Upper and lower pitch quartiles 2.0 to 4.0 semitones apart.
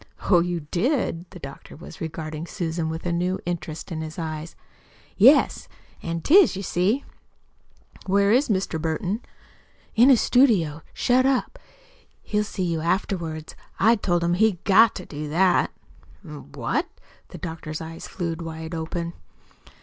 Yes: average, 3.7 semitones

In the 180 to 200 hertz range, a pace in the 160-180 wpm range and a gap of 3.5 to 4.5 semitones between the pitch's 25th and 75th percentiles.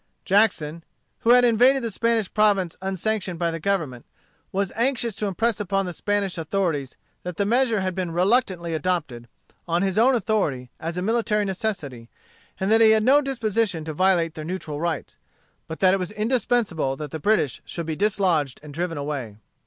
No: high, 190 Hz; average, 175 wpm; average, 5.0 semitones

